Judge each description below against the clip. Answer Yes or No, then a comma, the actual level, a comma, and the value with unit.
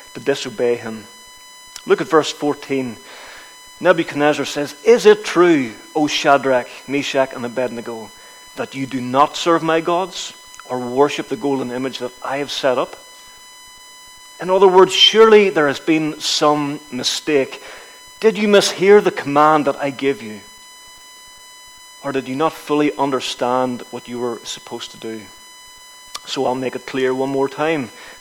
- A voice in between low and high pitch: Yes, medium, 150 Hz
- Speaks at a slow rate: No, average, 155 wpm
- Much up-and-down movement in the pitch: Yes, wide, 8.4 semitones